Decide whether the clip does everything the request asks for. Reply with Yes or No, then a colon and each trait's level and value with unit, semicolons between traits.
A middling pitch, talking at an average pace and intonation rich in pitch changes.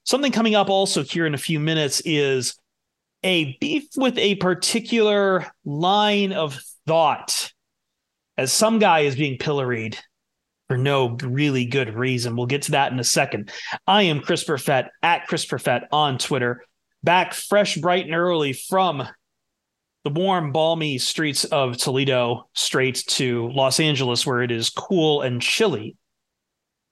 Yes: medium, 150 Hz; average, 150 wpm; wide, 6.0 semitones